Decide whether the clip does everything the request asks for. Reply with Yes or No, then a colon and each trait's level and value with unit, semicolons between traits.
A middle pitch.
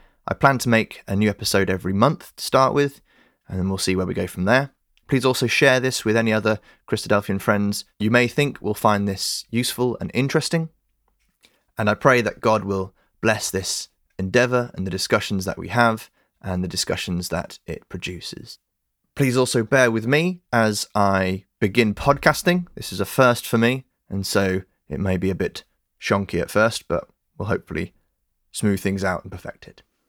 No: low, 110 Hz